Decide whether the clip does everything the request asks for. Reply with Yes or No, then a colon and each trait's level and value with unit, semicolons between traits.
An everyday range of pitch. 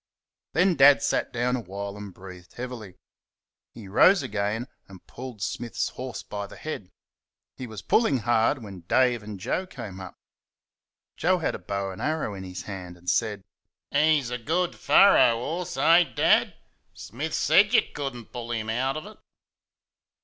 No: wide, 6.2 semitones